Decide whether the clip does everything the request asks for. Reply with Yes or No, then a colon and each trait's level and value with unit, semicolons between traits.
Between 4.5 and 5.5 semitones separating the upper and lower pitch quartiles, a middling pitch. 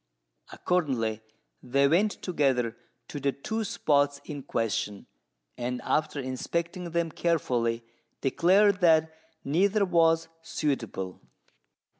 Yes: average, 5.1 semitones; medium, 150 Hz